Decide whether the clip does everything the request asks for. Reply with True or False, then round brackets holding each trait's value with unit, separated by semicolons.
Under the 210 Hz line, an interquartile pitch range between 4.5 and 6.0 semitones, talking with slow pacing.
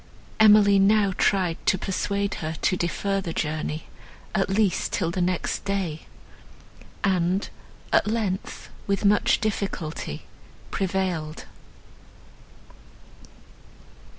False (190 Hz; 2.8 semitones; 95 wpm)